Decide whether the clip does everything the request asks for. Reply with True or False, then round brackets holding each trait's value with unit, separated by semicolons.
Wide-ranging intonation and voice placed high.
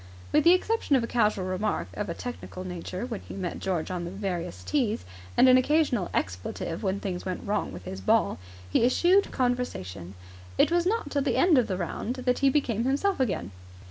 True (6.8 semitones; 215 Hz)